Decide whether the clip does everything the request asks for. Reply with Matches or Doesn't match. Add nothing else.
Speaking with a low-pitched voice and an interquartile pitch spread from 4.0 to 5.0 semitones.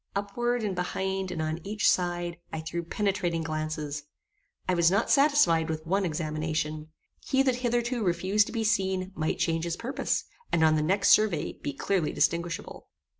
Doesn't match